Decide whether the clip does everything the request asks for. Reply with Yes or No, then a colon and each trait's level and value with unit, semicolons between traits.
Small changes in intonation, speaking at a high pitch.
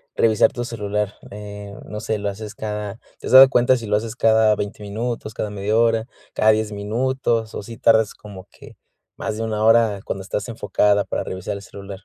No: narrow, 1.7 semitones; low, 105 Hz